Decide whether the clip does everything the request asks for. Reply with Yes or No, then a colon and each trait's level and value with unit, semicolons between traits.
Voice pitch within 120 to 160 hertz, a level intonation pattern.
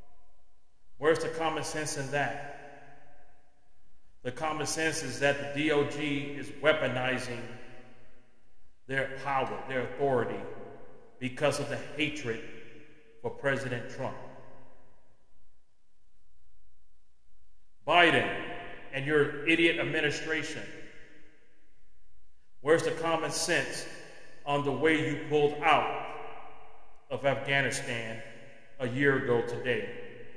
No: medium, 140 Hz; average, 3.9 semitones